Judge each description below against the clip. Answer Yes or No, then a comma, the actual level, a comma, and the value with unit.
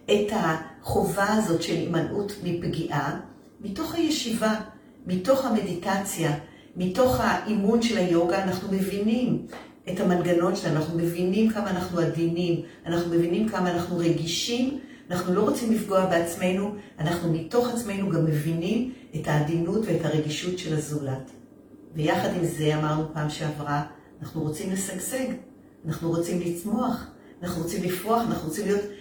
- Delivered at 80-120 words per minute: No, average, 130 wpm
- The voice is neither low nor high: Yes, medium, 180 Hz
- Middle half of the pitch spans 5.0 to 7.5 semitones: No, average, 4.0 semitones